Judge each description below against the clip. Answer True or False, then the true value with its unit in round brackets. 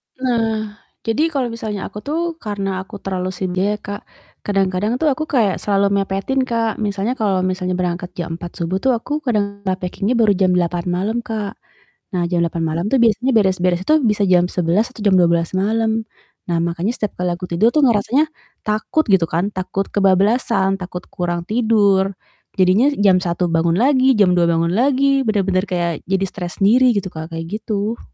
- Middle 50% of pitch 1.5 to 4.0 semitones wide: True (3.7 semitones)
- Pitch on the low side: False (195 Hz)